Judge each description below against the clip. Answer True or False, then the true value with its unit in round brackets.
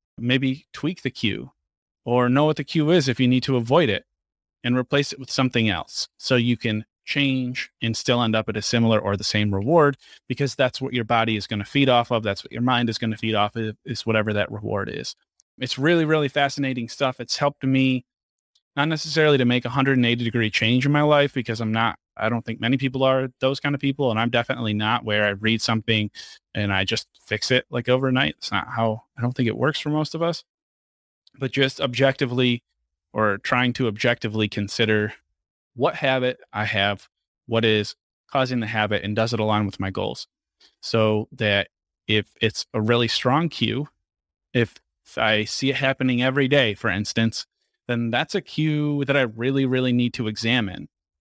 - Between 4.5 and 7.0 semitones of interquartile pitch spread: False (3.5 semitones)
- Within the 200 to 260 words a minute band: True (205 wpm)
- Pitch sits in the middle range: False (120 Hz)